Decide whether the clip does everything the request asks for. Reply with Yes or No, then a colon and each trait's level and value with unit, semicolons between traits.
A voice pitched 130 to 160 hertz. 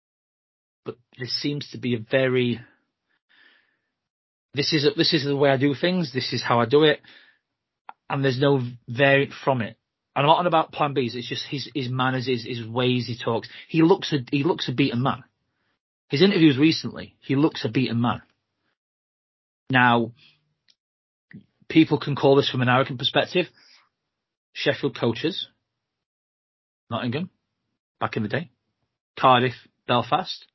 Yes: low, 135 Hz